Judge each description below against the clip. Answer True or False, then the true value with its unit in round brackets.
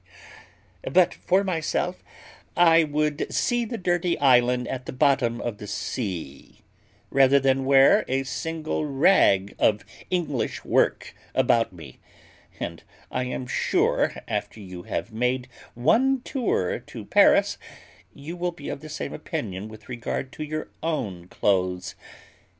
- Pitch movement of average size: False (6.3 semitones)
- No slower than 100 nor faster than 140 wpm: True (135 wpm)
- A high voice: False (135 Hz)